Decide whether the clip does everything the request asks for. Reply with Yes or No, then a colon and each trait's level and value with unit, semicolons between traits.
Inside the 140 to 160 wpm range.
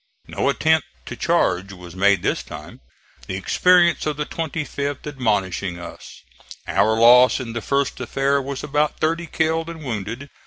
Yes: average, 155 wpm